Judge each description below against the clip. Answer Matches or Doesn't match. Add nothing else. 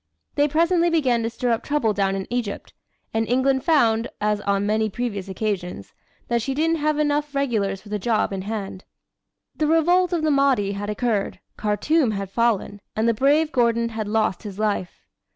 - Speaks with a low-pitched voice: Doesn't match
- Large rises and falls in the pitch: Matches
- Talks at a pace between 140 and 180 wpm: Doesn't match